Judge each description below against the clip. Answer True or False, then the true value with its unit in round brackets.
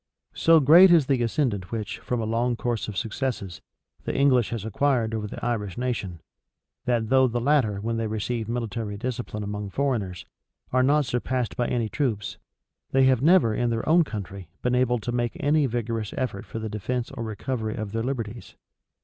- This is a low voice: True (120 Hz)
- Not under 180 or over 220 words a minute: True (185 wpm)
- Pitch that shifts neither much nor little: True (3.1 semitones)